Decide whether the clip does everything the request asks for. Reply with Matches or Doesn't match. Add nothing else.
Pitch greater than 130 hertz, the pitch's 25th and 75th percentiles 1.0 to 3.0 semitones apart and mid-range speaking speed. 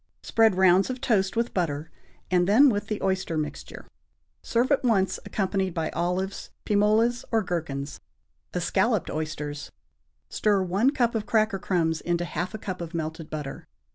Doesn't match